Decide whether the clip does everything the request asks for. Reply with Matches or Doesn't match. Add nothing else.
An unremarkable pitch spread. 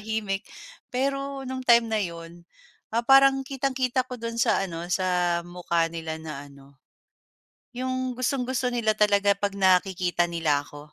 Doesn't match